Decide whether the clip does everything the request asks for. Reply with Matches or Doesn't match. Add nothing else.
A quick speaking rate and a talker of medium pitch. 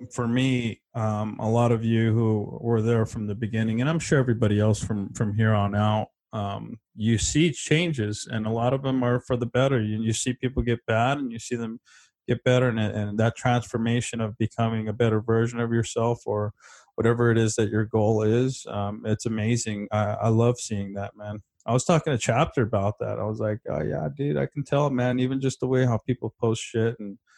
Doesn't match